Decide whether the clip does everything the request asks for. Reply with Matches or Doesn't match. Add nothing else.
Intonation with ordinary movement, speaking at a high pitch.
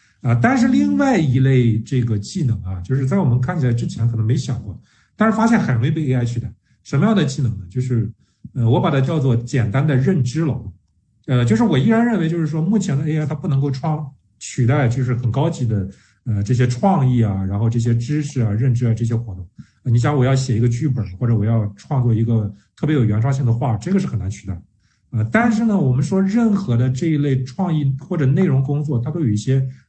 Doesn't match